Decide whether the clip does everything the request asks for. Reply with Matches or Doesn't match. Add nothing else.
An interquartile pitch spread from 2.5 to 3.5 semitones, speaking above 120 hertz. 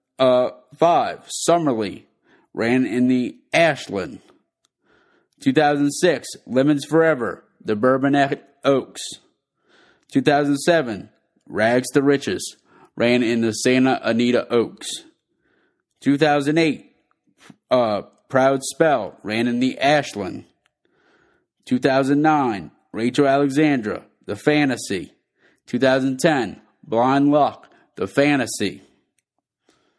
Matches